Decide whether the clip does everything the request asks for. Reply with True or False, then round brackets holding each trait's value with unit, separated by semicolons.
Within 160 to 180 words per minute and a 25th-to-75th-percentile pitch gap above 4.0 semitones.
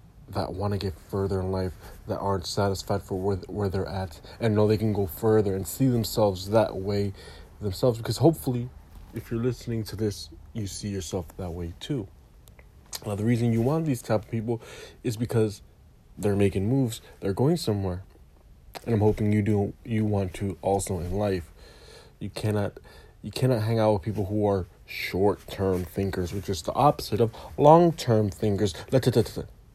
False (175 wpm; 3.0 semitones)